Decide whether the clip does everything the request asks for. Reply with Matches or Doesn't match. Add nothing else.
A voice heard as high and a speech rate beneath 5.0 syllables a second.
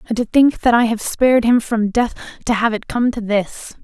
Doesn't match